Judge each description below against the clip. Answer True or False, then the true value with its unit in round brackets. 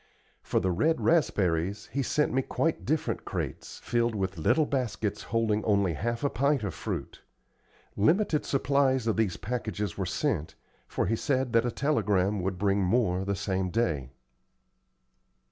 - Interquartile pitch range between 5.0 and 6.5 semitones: True (5.6 semitones)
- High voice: False (110 Hz)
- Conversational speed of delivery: True (155 wpm)